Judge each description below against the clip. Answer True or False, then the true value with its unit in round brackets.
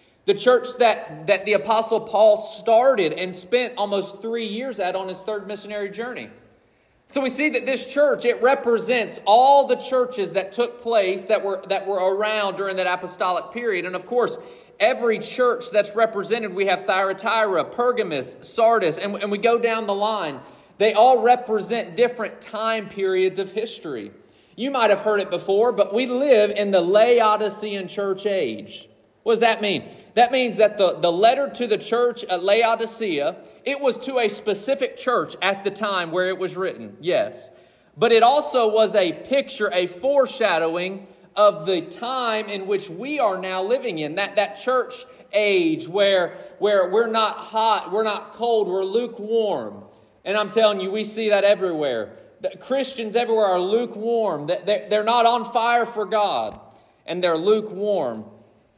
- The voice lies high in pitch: True (215 Hz)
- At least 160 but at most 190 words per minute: True (170 wpm)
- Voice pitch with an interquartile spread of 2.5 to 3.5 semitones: True (3.2 semitones)